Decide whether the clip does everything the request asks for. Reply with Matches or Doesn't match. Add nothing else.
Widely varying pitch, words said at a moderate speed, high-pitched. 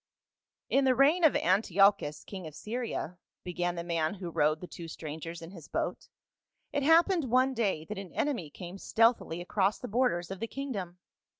Matches